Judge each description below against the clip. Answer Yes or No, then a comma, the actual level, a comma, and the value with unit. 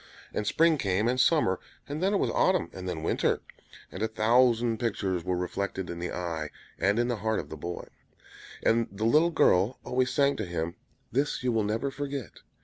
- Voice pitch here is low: Yes, low, 110 Hz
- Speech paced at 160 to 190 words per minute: No, average, 200 wpm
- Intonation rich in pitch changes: Yes, wide, 5.8 semitones